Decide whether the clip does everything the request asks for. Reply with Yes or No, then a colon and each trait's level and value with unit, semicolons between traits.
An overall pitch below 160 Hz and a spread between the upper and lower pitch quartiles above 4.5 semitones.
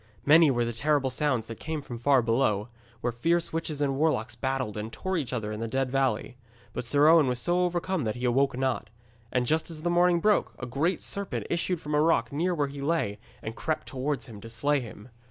Yes: low, 135 Hz; average, 5.1 semitones